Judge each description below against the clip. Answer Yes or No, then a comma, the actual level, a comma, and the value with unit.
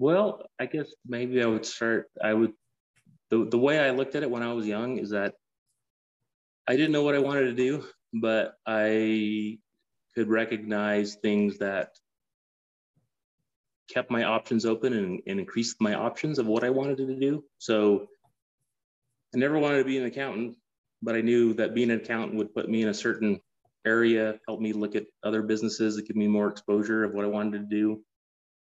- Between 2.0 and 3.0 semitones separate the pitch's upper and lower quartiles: Yes, narrow, 2.5 semitones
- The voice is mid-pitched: No, low, 110 Hz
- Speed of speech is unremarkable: Yes, average, 190 wpm